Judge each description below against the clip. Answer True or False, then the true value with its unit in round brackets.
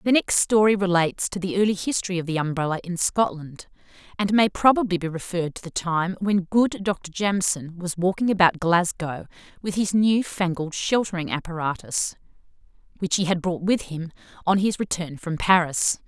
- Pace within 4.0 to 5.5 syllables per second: True (5.2 syllables/s)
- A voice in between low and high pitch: True (180 Hz)